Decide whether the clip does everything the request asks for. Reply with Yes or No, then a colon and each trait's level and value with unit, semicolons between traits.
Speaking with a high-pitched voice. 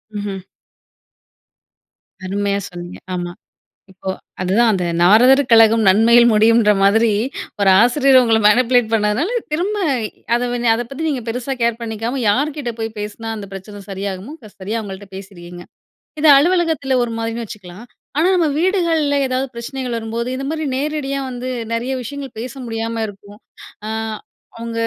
Yes: high, 230 Hz